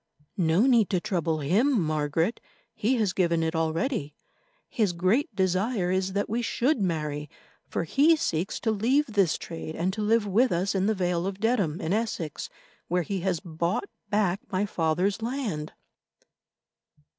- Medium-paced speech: Yes, average, 160 wpm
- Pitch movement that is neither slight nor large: Yes, average, 4.9 semitones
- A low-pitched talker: No, high, 190 Hz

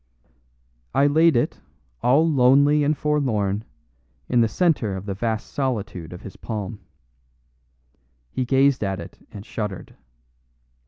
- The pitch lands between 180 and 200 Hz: No, low, 120 Hz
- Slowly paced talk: Yes, slow, 125 wpm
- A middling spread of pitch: No, wide, 5.7 semitones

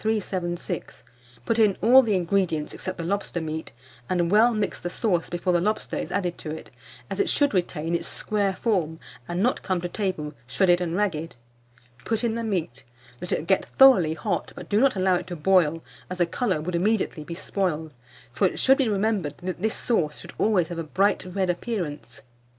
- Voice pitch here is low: No, medium, 185 Hz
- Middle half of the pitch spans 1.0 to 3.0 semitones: No, average, 3.8 semitones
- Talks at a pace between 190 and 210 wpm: Yes, average, 200 wpm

